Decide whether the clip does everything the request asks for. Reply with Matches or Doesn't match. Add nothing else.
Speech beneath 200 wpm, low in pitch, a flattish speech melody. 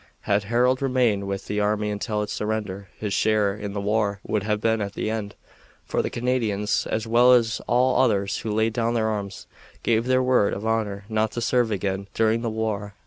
Doesn't match